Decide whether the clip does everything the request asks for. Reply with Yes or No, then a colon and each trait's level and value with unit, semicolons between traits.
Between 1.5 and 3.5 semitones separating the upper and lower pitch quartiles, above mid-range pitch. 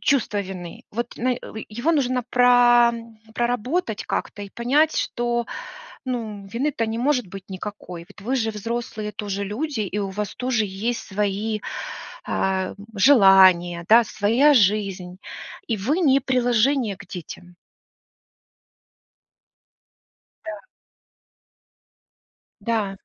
No: average, 3.9 semitones; high, 220 Hz